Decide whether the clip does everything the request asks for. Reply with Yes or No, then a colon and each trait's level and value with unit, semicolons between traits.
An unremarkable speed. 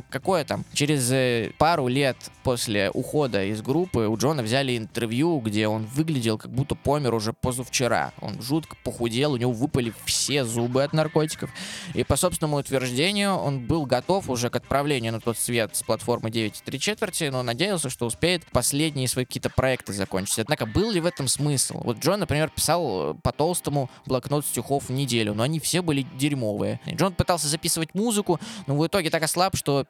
No: fast, 180 wpm